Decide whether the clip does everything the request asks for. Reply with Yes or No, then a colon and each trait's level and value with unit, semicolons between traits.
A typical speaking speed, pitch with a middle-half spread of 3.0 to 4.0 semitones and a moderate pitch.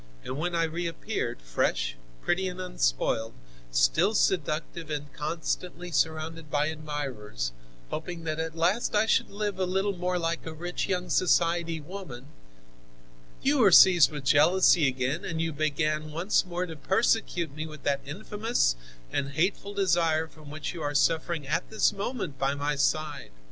Yes: average, 160 wpm; average, 3.5 semitones; medium, 160 Hz